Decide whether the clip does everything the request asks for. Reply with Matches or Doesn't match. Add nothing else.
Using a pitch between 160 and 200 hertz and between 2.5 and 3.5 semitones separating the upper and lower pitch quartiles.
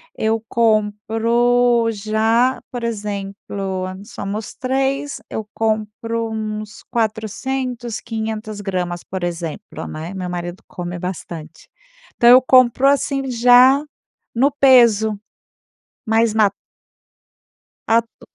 Doesn't match